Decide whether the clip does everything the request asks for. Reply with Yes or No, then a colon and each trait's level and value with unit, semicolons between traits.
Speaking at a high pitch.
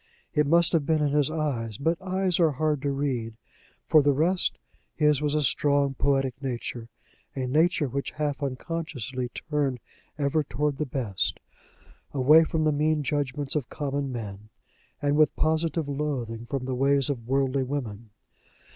No: medium, 140 Hz